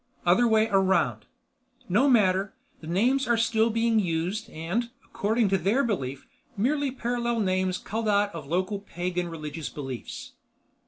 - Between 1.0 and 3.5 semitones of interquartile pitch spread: No, average, 4.7 semitones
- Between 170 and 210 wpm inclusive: No, average, 145 wpm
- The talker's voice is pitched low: No, high, 200 Hz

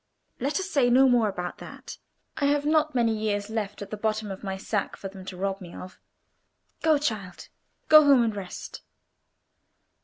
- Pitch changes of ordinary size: No, wide, 6.1 semitones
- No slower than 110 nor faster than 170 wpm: No, average, 185 wpm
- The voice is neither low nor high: No, high, 215 Hz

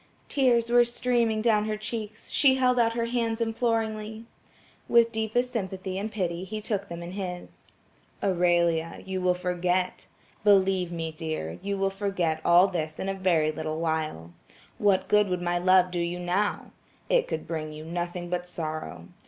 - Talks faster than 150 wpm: Yes, average, 170 wpm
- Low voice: No, high, 190 Hz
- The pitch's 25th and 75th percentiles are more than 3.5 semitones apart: Yes, average, 4.1 semitones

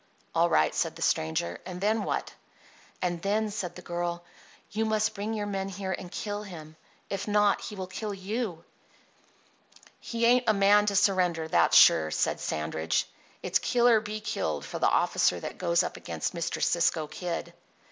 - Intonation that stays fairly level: No, average, 3.6 semitones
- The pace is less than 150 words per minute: No, average, 180 wpm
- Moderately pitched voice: No, high, 195 Hz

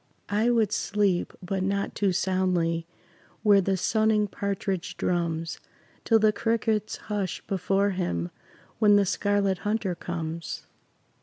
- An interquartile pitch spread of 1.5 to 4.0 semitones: Yes, average, 2.8 semitones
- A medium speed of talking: No, slow, 125 wpm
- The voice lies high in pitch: Yes, high, 195 Hz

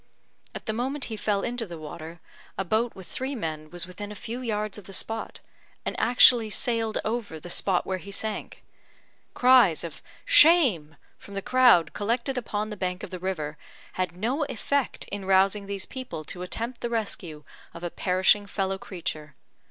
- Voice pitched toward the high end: Yes, high, 205 Hz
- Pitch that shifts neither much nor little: Yes, average, 4.7 semitones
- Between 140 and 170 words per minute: No, average, 180 wpm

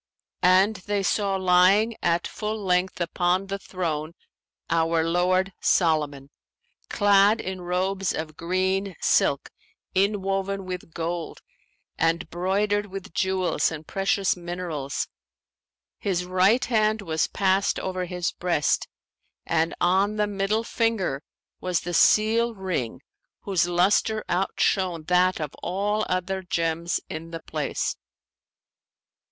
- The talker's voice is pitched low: No, medium, 185 Hz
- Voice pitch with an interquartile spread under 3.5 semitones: Yes, narrow, 2.6 semitones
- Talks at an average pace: No, slow, 115 wpm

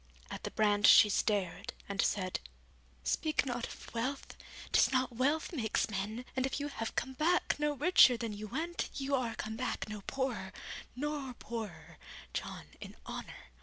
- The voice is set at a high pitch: Yes, high, 245 Hz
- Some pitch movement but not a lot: Yes, average, 4.6 semitones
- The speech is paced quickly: No, average, 165 wpm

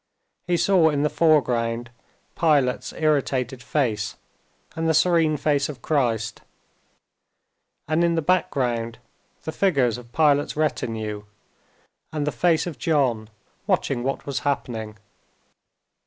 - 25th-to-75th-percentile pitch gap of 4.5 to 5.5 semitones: Yes, average, 4.8 semitones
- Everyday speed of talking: No, slow, 120 wpm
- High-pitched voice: No, medium, 140 Hz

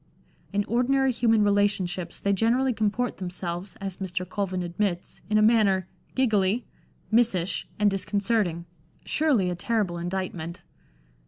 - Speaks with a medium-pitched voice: No, high, 200 Hz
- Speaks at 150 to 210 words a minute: No, average, 140 wpm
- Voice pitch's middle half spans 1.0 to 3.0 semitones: No, average, 3.7 semitones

